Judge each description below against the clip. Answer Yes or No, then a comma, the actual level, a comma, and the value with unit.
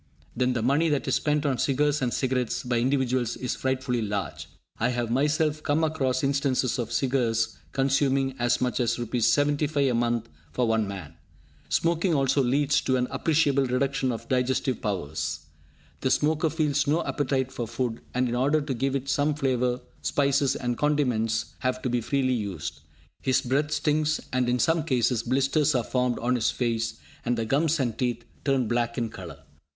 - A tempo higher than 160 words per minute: Yes, average, 180 wpm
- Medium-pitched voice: No, low, 130 Hz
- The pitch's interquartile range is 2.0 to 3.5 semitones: Yes, average, 2.9 semitones